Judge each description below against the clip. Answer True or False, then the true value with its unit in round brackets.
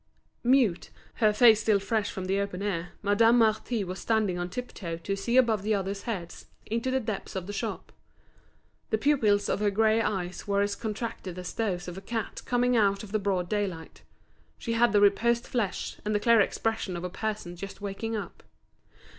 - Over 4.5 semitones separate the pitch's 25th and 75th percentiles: False (2.7 semitones)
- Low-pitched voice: False (205 Hz)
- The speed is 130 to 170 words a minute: False (195 wpm)